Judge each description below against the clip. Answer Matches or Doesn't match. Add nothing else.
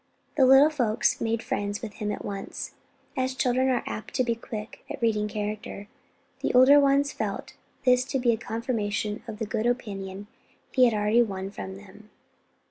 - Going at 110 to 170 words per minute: Doesn't match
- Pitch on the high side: Matches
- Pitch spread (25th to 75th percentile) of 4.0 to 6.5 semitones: Doesn't match